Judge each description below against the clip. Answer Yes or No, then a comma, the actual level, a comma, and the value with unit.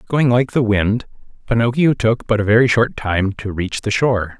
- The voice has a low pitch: Yes, low, 115 Hz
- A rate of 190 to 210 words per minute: Yes, fast, 205 wpm